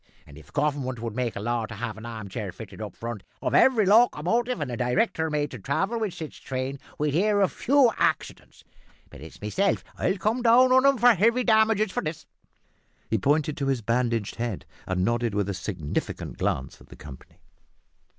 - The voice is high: No, medium, 140 Hz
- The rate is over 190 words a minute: Yes, average, 200 wpm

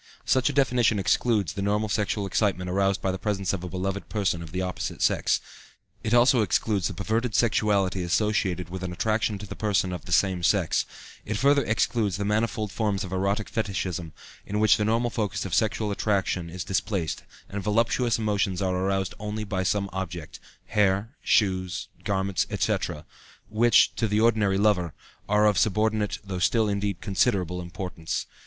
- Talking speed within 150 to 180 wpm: Yes, average, 175 wpm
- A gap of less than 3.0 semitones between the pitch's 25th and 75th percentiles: Yes, narrow, 2.6 semitones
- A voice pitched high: No, low, 100 Hz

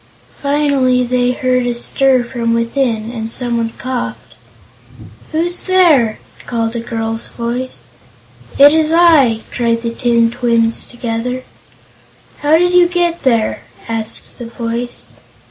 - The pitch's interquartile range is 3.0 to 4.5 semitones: Yes, average, 3.4 semitones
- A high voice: Yes, high, 245 Hz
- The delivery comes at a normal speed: No, slow, 120 wpm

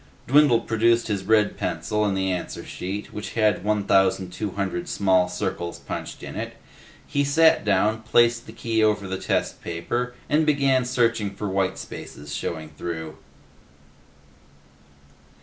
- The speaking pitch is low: Yes, low, 105 Hz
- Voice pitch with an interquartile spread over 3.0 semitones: Yes, average, 3.9 semitones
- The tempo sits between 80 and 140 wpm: Yes, slow, 135 wpm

